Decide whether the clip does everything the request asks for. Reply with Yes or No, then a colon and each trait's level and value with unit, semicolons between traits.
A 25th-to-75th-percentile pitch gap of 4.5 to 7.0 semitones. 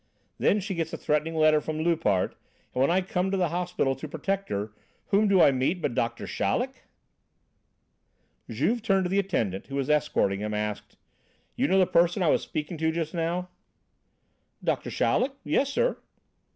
Yes: average, 5.2 semitones